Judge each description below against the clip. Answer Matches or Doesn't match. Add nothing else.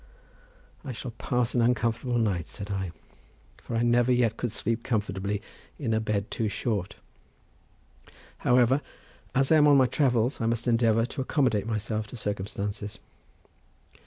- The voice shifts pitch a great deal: Doesn't match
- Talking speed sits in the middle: Matches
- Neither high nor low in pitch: Doesn't match